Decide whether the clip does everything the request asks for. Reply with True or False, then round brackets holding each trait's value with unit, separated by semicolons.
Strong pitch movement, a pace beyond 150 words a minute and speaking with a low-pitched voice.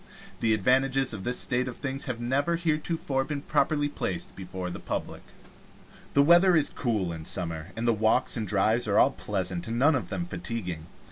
True (6.3 semitones; 190 wpm; 120 Hz)